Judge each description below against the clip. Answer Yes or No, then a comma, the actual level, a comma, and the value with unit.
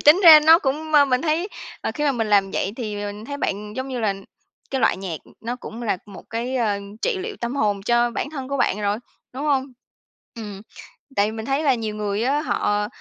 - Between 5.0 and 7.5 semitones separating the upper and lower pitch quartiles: Yes, wide, 5.4 semitones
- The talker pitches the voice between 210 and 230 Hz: No, high, 240 Hz